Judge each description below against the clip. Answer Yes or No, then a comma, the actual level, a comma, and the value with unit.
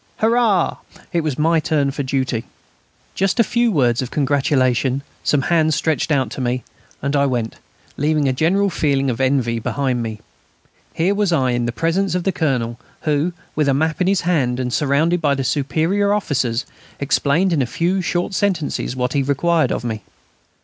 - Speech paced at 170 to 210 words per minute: Yes, average, 185 wpm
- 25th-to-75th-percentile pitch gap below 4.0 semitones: No, average, 4.9 semitones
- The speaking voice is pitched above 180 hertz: No, medium, 145 Hz